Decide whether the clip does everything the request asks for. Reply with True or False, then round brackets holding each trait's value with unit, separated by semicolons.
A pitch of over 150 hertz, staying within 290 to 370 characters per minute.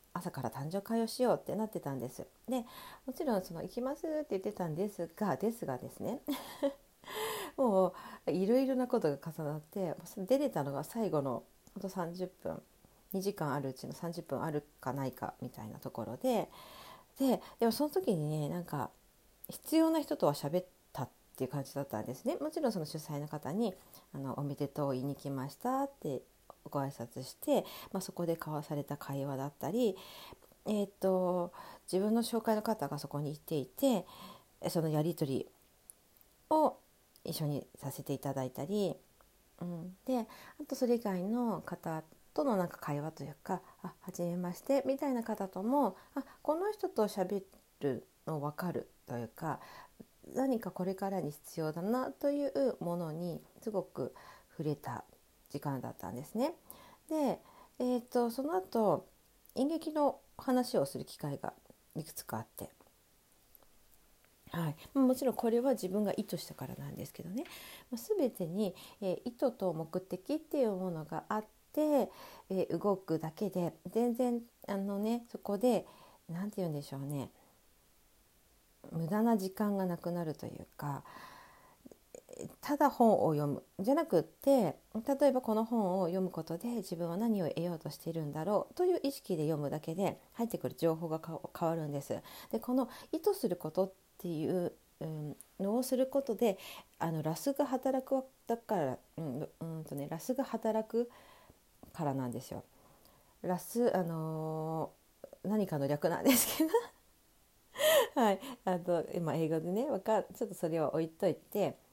True (190 Hz; 295 characters per minute)